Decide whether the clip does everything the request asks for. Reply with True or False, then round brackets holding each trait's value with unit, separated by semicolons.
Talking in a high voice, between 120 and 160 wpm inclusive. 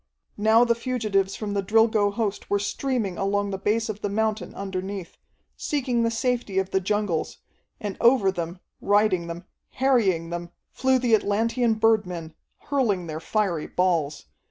True (205 Hz; 155 wpm)